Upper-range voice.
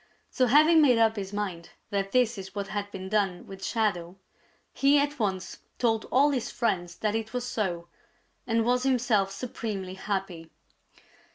Yes: high, 210 Hz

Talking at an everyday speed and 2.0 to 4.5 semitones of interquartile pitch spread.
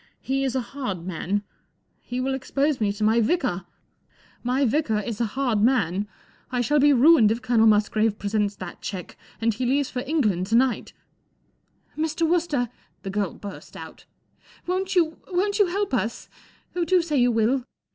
No: average, 190 wpm; wide, 5.6 semitones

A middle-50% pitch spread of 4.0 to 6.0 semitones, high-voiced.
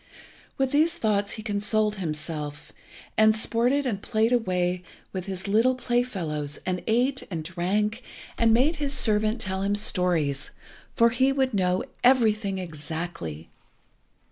Yes: average, 4.9 semitones; high, 210 Hz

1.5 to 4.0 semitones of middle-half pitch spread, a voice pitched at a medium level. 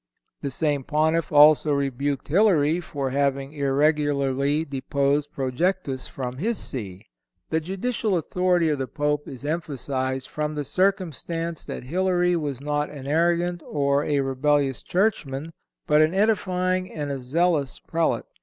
Yes: average, 3.6 semitones; medium, 150 Hz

